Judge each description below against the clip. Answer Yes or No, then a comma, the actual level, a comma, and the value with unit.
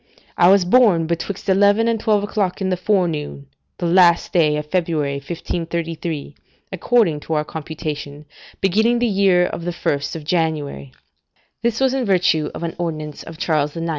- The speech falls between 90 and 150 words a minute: No, average, 165 wpm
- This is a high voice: No, medium, 170 Hz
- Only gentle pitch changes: No, average, 4.2 semitones